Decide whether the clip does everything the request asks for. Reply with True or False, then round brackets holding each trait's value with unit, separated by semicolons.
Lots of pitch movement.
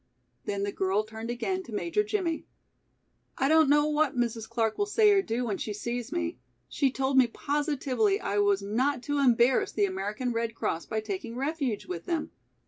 True (5.7 semitones)